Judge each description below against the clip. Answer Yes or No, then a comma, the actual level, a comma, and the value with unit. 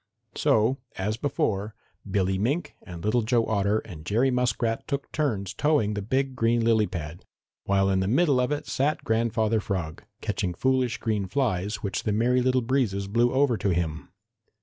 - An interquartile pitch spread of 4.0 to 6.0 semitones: Yes, average, 4.5 semitones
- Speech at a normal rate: Yes, average, 170 wpm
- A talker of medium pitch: No, low, 110 Hz